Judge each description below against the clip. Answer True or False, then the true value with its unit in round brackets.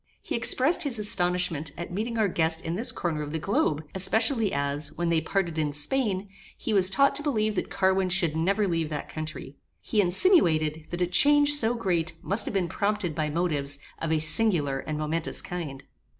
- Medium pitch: True (175 Hz)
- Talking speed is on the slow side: False (195 wpm)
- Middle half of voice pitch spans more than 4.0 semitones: True (5.1 semitones)